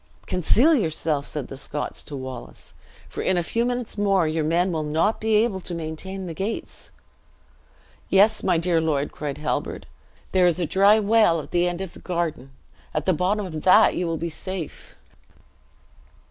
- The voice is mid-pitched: Yes, medium, 175 Hz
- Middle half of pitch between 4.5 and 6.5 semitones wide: No, average, 4.0 semitones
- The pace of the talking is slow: No, average, 180 wpm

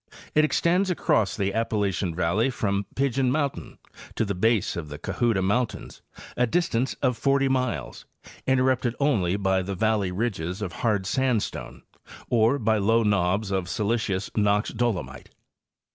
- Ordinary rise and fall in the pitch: Yes, average, 4.7 semitones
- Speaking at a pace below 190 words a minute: Yes, average, 145 wpm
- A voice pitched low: Yes, low, 110 Hz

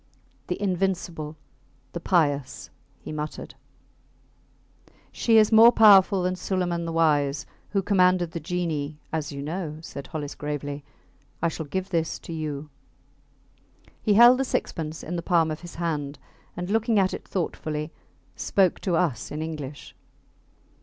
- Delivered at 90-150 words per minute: Yes, average, 145 wpm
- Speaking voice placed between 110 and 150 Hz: No, medium, 165 Hz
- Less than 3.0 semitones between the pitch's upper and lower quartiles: No, average, 3.6 semitones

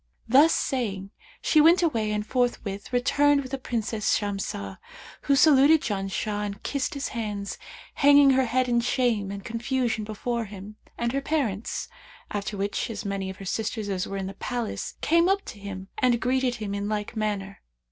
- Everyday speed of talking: Yes, average, 180 wpm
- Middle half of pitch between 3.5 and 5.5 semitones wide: Yes, average, 4.6 semitones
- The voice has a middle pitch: No, high, 225 Hz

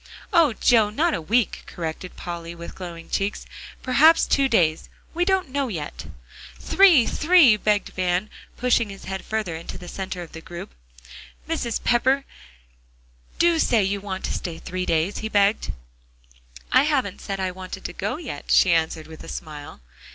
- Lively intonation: Yes, wide, 6.8 semitones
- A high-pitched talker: Yes, high, 200 Hz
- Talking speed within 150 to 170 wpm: Yes, average, 165 wpm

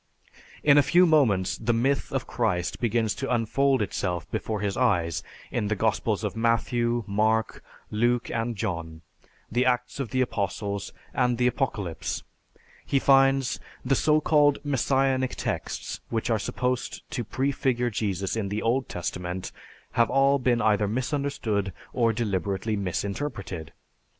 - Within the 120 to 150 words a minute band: Yes, average, 140 wpm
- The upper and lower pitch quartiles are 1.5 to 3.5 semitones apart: No, average, 4.4 semitones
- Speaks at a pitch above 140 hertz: No, low, 115 Hz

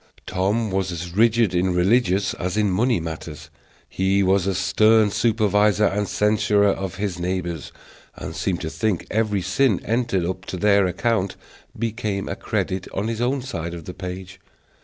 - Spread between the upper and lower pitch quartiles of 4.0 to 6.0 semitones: No, average, 2.9 semitones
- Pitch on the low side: Yes, low, 100 Hz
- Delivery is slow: No, average, 165 wpm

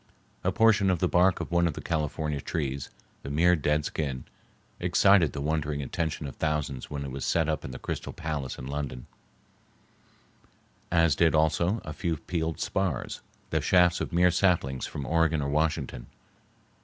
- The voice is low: Yes, very low, 80 Hz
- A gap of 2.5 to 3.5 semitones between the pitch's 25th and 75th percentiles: Yes, average, 3.2 semitones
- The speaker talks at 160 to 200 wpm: Yes, average, 170 wpm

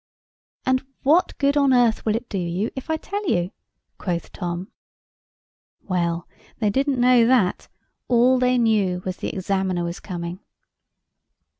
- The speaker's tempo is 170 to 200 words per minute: No, average, 150 wpm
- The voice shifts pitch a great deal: Yes, wide, 6.0 semitones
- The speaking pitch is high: Yes, high, 215 Hz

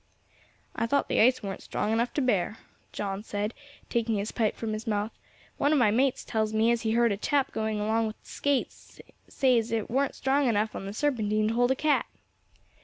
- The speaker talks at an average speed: No, fast, 210 wpm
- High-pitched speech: Yes, high, 225 Hz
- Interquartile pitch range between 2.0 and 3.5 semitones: Yes, average, 3.0 semitones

